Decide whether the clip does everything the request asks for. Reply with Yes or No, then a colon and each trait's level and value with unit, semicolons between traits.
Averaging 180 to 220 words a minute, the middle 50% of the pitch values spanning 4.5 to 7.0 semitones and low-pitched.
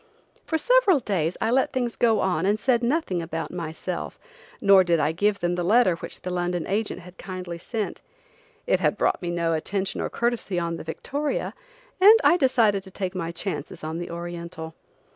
No: average, 190 wpm; average, 5.3 semitones; medium, 185 Hz